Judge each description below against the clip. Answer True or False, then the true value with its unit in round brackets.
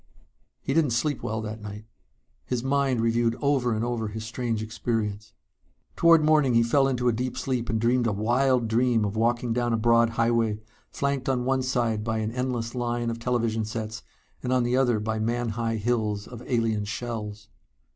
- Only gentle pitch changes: True (2.1 semitones)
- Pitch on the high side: False (115 Hz)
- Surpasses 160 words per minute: True (185 wpm)